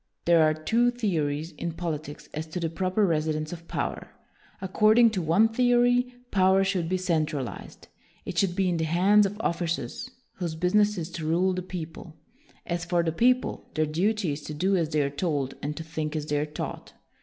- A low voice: No, medium, 170 Hz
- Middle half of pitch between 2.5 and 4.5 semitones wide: Yes, average, 3.7 semitones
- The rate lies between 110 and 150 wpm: No, fast, 205 wpm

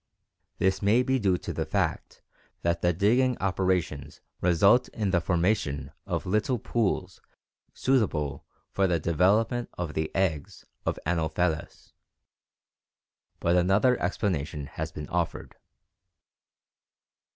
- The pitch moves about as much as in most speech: Yes, average, 4.1 semitones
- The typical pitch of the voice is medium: No, very low, 90 Hz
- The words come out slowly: Yes, slow, 115 wpm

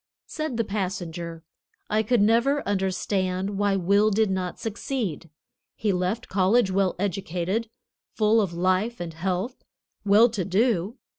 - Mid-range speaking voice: No, high, 195 Hz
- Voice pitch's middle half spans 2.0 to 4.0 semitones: Yes, average, 3.2 semitones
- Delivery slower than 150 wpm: Yes, slow, 135 wpm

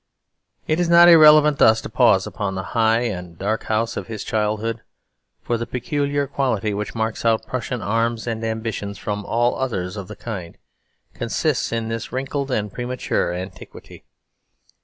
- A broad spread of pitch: No, average, 3.2 semitones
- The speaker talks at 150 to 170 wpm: Yes, average, 160 wpm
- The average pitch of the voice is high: No, low, 115 Hz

